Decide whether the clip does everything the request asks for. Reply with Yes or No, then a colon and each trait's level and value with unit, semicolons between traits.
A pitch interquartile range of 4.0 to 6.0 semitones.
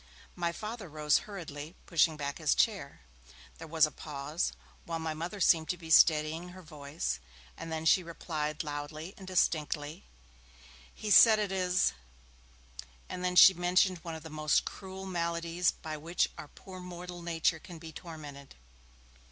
No: average, 2.9 semitones